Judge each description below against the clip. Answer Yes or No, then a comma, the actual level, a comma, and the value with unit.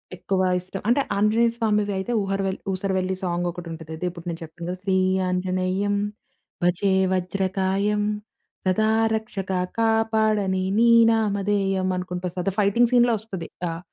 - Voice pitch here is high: Yes, high, 195 Hz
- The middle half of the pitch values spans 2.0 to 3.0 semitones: Yes, narrow, 2.5 semitones